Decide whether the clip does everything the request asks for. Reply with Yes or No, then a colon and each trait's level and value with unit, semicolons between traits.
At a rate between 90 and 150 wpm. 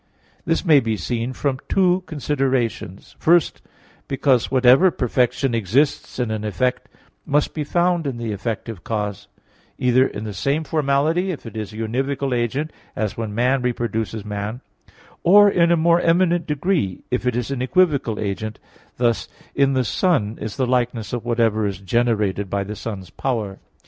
No: average, 165 wpm